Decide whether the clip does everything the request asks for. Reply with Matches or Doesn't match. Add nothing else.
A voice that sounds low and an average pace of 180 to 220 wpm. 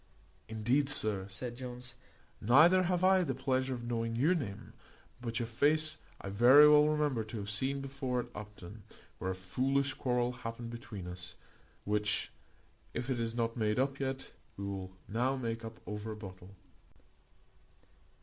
Doesn't match